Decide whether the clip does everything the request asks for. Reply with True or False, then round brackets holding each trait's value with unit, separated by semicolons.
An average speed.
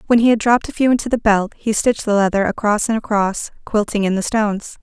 False (250 wpm)